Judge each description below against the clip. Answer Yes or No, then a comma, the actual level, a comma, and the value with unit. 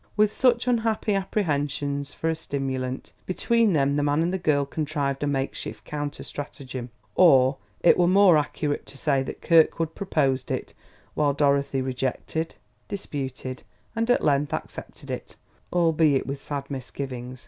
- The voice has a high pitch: No, medium, 145 Hz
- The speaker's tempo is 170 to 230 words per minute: No, average, 150 wpm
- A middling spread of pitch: Yes, average, 3.6 semitones